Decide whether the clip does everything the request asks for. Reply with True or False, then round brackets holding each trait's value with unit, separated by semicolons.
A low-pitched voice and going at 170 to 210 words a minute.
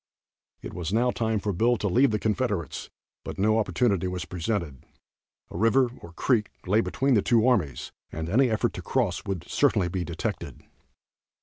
True (105 Hz; 175 wpm)